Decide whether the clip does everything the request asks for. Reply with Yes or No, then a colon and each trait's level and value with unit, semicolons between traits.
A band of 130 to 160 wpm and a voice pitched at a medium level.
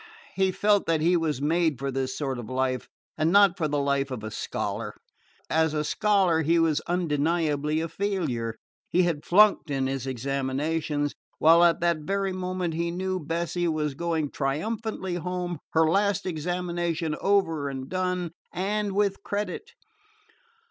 Yes: average, 155 wpm; medium, 165 Hz